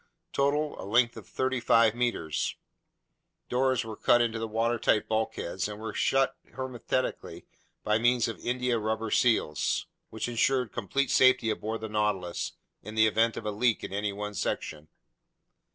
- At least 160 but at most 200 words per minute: No, average, 150 wpm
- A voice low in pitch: Yes, low, 115 Hz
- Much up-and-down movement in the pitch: No, narrow, 2.6 semitones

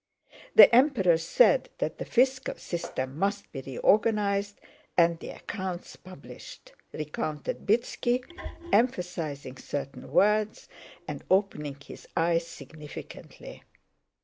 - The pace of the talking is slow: Yes, slow, 100 wpm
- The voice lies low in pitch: No, medium, 185 Hz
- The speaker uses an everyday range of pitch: No, wide, 5.9 semitones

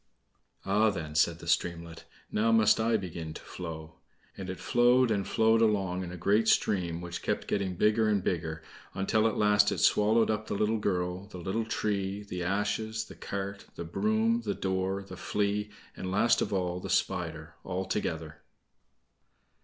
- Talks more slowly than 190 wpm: Yes, average, 175 wpm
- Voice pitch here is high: No, low, 100 Hz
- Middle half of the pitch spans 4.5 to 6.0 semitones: No, average, 3.2 semitones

